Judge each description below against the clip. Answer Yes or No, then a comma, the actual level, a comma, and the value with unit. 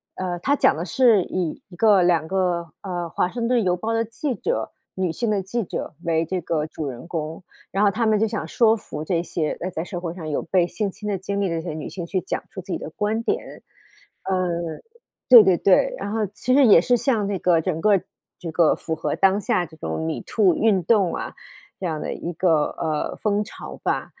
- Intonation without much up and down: No, average, 4.0 semitones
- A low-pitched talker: No, medium, 185 Hz